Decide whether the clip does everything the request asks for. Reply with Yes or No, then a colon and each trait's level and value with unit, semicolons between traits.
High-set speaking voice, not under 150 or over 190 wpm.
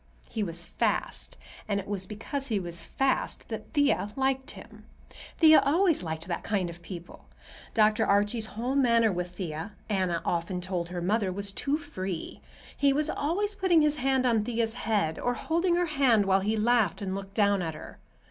Yes: high, 210 Hz; average, 185 wpm